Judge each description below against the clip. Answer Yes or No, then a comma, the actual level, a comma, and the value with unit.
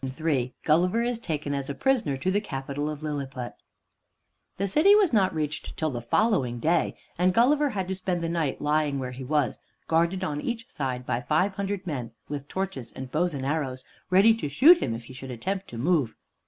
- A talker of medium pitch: Yes, medium, 155 Hz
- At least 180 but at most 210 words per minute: Yes, fast, 205 wpm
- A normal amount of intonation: No, wide, 6.1 semitones